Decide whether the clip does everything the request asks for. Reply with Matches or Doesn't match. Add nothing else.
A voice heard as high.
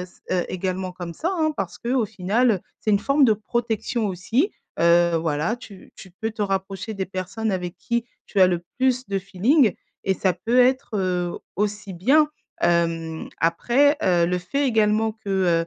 Matches